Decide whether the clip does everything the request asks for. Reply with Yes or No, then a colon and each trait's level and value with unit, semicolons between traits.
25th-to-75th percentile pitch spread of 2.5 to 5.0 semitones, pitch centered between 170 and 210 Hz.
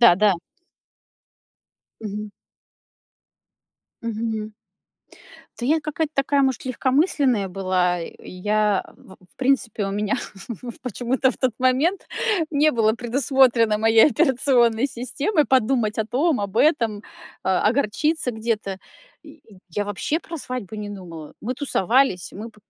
No: average, 4.3 semitones; high, 230 Hz